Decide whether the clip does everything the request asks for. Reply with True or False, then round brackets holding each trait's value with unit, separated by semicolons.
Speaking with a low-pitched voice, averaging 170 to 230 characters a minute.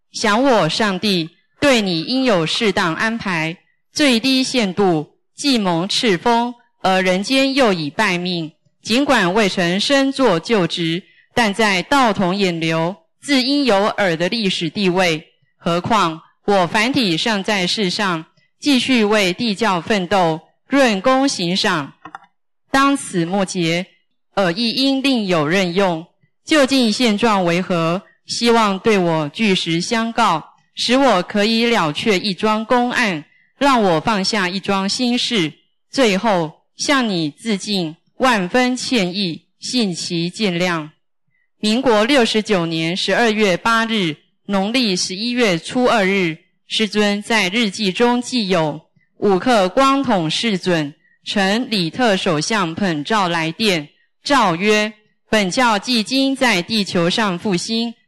False (205 Hz; 185 characters per minute)